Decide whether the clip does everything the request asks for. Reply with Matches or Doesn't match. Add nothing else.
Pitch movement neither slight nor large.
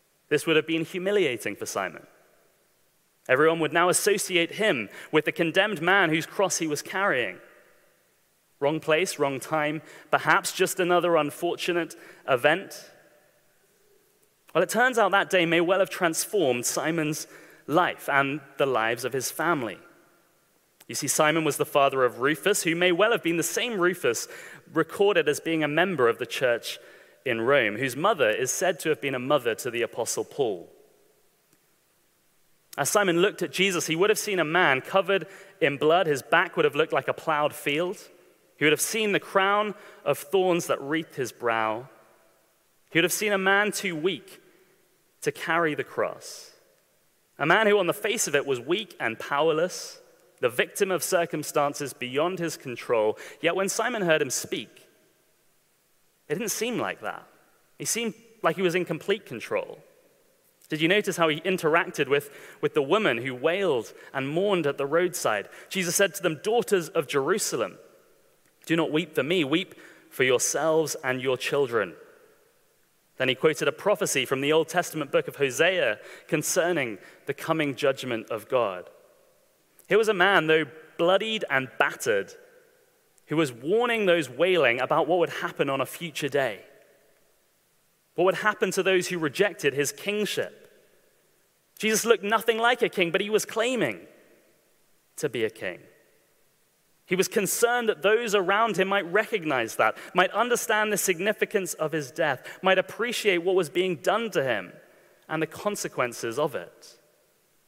Doesn't match